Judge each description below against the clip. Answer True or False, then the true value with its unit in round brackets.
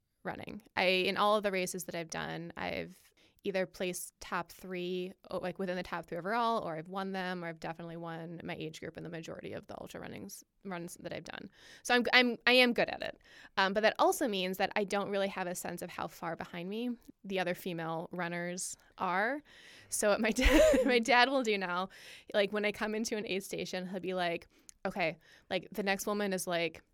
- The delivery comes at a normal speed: False (225 wpm)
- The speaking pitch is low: False (190 Hz)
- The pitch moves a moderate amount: True (3.3 semitones)